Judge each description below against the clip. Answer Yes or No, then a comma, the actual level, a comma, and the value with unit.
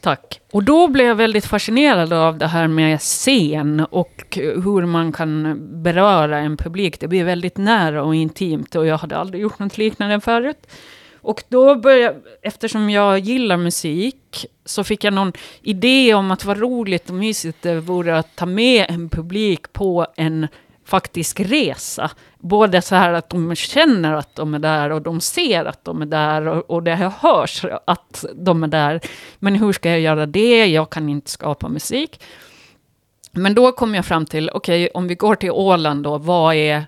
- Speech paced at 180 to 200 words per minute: Yes, average, 185 wpm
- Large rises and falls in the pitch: No, average, 4.8 semitones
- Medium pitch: Yes, medium, 180 Hz